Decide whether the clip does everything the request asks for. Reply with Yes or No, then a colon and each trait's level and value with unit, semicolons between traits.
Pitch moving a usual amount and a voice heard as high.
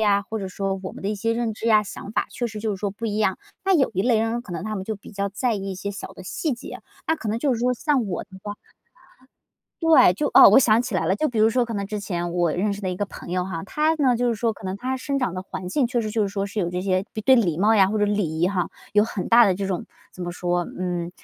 Yes: average, 3.8 semitones; high, 205 Hz